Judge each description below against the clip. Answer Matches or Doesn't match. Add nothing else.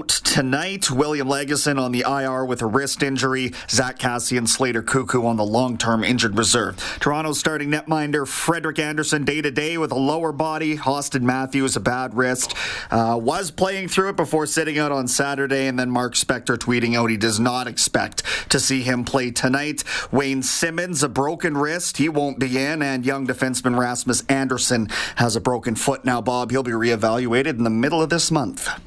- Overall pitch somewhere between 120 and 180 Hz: Matches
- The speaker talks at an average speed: Matches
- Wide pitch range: Doesn't match